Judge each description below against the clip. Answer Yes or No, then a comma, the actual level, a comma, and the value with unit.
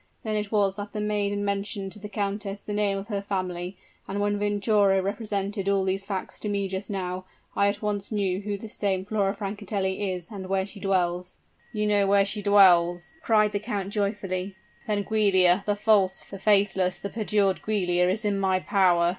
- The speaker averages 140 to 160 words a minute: No, average, 195 wpm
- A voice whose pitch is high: Yes, high, 200 Hz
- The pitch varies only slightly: Yes, narrow, 1.4 semitones